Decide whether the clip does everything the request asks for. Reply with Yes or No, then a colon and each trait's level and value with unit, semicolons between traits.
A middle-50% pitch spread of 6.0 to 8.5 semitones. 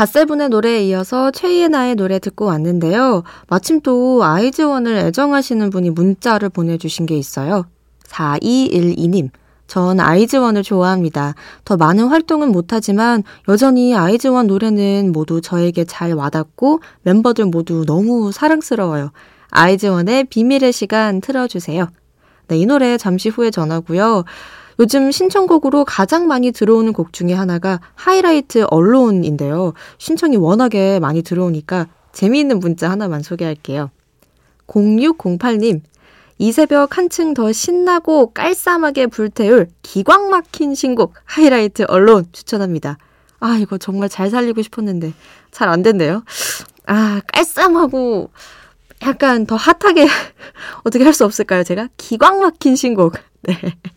Yes: wide, 6.5 semitones